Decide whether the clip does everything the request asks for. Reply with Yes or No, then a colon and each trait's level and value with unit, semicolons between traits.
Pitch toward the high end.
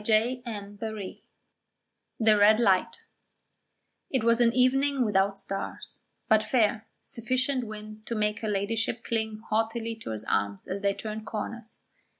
Yes: high, 220 Hz